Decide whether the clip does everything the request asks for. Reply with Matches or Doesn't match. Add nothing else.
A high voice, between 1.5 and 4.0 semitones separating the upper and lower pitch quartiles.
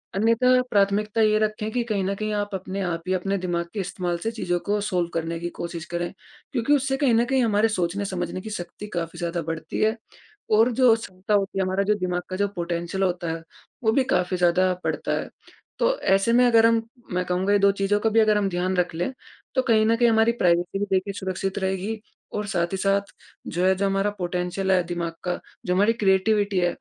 Matches